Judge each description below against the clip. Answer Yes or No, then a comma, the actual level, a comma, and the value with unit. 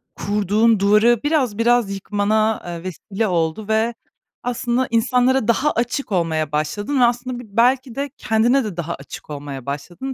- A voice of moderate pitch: No, high, 220 Hz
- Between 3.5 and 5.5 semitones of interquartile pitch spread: Yes, average, 5.0 semitones